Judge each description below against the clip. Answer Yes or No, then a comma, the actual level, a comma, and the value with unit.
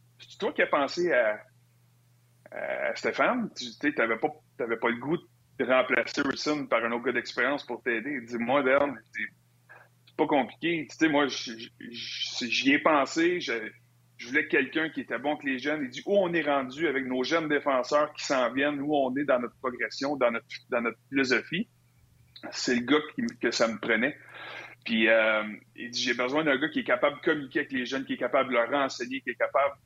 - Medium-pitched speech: No, low, 130 Hz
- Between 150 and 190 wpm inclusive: No, average, 215 wpm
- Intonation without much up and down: No, average, 3.8 semitones